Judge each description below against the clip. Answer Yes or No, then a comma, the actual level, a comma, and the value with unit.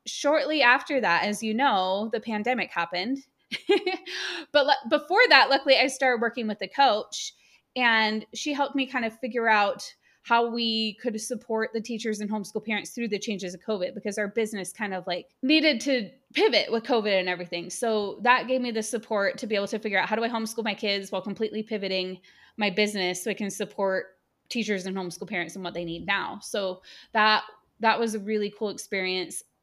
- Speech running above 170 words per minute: Yes, average, 200 wpm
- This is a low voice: No, high, 220 Hz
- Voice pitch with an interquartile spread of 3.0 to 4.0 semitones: Yes, average, 3.6 semitones